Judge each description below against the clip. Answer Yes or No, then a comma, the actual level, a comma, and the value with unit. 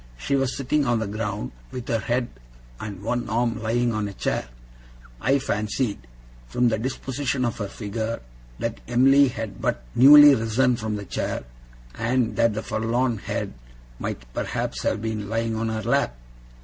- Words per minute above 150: Yes, average, 165 wpm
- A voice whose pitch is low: Yes, low, 115 Hz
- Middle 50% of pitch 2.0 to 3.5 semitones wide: Yes, average, 2.7 semitones